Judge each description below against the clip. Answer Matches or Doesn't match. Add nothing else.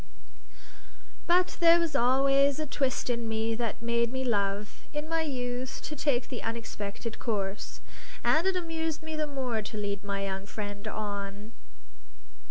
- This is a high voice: Matches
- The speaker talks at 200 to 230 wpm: Doesn't match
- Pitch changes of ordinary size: Doesn't match